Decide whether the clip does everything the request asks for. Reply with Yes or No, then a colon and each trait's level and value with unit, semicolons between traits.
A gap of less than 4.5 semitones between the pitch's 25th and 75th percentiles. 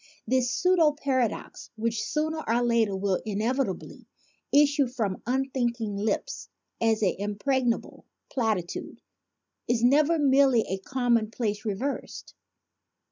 Yes: average, 4.0 semitones